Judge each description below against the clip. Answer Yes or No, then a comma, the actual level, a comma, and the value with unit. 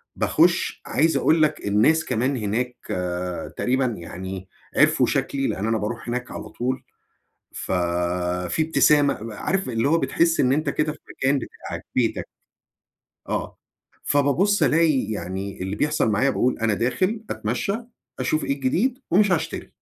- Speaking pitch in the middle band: No, low, 125 Hz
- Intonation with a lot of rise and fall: Yes, wide, 7.2 semitones